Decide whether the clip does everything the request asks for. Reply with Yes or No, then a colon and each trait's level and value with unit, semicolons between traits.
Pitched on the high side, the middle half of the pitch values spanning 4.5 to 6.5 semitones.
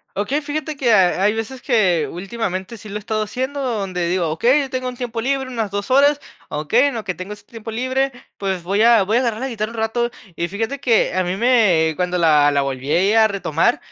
Yes: high, 220 Hz; average, 5.2 semitones